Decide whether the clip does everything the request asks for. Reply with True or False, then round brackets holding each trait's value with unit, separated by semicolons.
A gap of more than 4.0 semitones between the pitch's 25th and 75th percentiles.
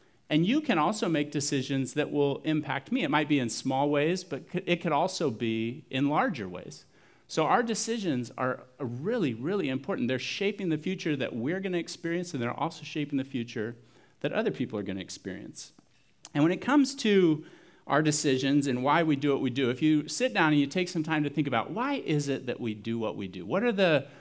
True (4.4 semitones)